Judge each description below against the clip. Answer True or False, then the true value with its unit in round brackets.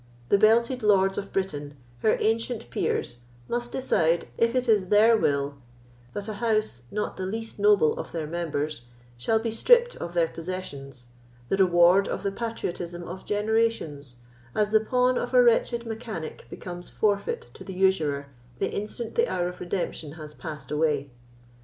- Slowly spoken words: False (165 wpm)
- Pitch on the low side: False (195 Hz)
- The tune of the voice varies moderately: False (5.7 semitones)